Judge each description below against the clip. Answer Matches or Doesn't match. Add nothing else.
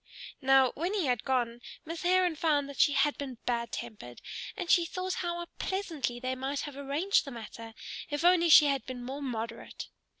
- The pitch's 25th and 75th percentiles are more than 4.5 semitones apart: Matches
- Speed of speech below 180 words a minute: Doesn't match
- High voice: Matches